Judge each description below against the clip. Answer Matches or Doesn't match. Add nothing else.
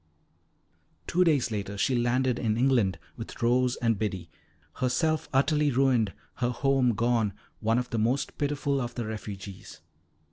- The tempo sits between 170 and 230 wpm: Doesn't match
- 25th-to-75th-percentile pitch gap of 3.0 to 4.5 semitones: Matches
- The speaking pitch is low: Matches